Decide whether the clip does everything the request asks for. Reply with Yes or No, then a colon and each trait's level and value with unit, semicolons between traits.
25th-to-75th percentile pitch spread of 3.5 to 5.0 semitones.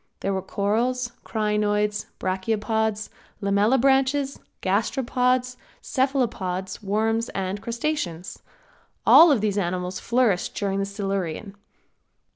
Yes: average, 4.1 semitones